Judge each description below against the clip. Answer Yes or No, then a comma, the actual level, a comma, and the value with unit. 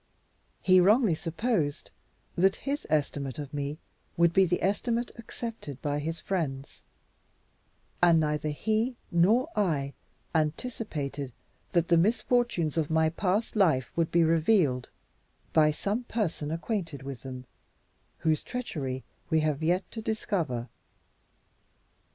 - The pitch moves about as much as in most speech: No, wide, 5.8 semitones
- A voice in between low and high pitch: Yes, medium, 165 Hz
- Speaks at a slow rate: Yes, slow, 120 wpm